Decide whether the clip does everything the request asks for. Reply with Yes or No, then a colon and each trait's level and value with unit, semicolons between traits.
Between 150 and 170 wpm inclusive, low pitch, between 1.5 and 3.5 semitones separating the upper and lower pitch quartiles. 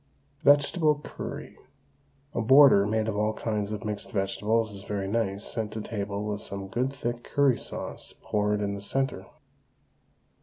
Yes: average, 155 wpm; low, 105 Hz; average, 2.8 semitones